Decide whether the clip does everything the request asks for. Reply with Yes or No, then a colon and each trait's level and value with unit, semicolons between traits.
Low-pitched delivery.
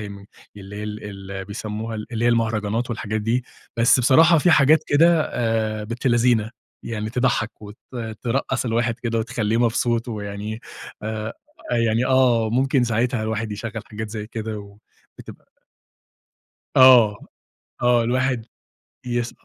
Yes: low, 115 Hz